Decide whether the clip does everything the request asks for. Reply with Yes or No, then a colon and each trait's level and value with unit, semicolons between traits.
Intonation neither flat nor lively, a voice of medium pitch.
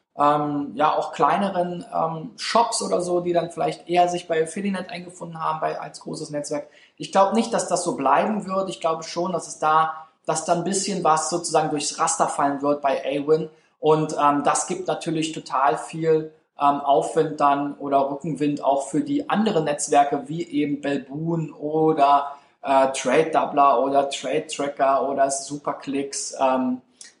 Yes: average, 3.0 semitones; medium, 155 Hz